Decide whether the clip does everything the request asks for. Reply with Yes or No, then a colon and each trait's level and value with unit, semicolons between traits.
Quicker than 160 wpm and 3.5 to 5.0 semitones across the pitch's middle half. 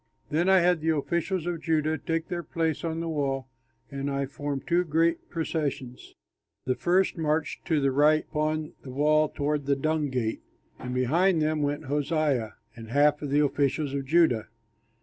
No: average, 175 wpm; average, 2.8 semitones